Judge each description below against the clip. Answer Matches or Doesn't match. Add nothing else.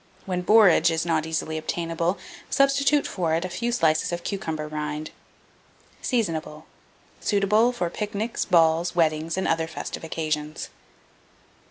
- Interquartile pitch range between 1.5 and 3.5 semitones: Doesn't match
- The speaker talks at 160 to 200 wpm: Doesn't match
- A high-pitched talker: Doesn't match